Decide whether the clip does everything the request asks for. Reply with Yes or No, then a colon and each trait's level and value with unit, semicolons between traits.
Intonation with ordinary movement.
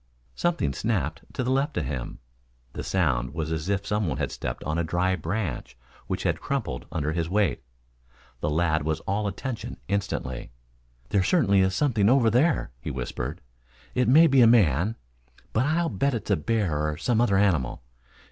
No: wide, 7.0 semitones